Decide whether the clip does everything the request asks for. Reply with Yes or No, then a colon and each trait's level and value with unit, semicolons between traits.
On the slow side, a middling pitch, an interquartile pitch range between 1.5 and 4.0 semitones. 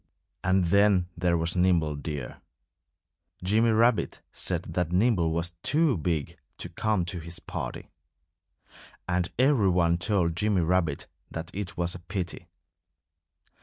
No: slow, 130 wpm; very low, 90 Hz; average, 3.1 semitones